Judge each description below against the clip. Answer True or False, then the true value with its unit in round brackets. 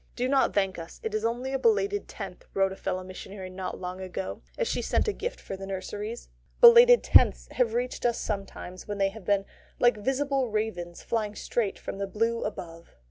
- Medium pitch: False (210 Hz)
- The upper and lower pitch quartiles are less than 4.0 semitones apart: False (4.5 semitones)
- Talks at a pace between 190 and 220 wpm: True (200 wpm)